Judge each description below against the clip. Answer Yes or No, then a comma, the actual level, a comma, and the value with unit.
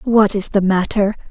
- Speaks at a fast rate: No, average, 185 wpm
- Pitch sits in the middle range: No, high, 205 Hz